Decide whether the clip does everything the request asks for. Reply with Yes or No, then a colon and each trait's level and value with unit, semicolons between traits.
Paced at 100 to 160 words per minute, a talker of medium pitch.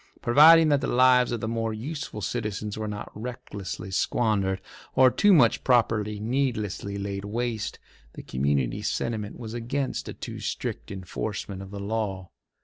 No: average, 150 wpm; low, 110 Hz